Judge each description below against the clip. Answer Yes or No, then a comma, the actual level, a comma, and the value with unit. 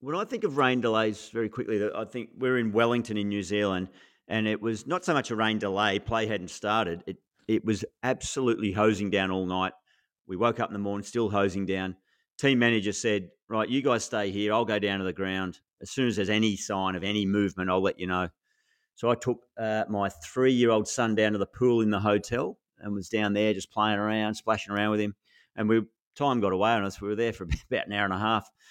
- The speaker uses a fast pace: Yes, fast, 240 wpm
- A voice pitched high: No, low, 105 Hz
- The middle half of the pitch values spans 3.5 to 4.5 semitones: No, narrow, 2.6 semitones